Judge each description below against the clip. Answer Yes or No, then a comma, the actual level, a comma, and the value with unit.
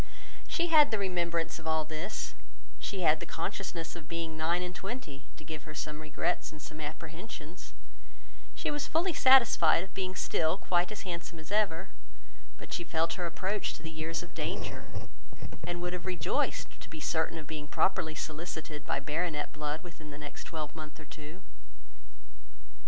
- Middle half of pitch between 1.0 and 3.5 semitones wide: Yes, average, 2.8 semitones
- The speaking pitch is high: No, medium, 165 Hz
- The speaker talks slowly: No, average, 175 wpm